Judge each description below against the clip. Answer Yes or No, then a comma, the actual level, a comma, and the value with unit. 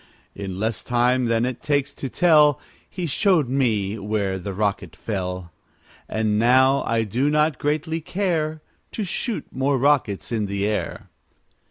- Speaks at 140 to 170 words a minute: Yes, average, 150 wpm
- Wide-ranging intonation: Yes, wide, 6.0 semitones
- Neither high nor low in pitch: No, low, 125 Hz